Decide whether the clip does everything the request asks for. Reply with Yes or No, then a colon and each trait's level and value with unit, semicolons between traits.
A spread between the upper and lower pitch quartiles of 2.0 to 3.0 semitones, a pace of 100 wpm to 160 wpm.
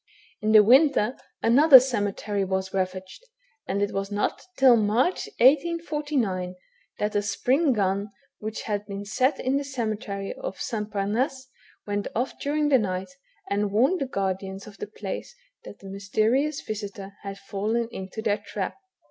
No: average, 4.7 semitones; average, 155 wpm